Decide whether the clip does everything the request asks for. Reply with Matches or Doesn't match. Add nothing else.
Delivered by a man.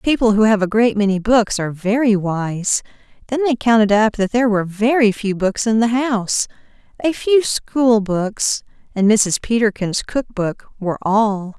Doesn't match